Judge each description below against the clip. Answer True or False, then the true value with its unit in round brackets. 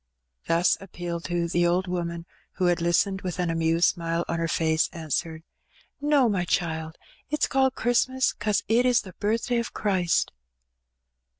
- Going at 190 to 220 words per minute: False (165 wpm)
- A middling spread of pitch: True (4.2 semitones)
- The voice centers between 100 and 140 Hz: False (175 Hz)